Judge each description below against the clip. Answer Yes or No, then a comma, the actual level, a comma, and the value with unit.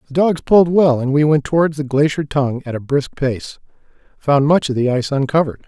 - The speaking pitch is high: No, medium, 140 Hz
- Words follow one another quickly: Yes, fast, 220 wpm